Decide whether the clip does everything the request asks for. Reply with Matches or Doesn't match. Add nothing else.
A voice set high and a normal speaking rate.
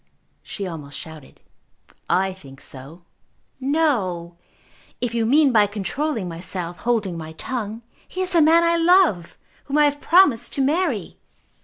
Matches